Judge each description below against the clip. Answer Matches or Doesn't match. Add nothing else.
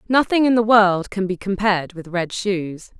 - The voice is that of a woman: Matches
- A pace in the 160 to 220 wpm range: Matches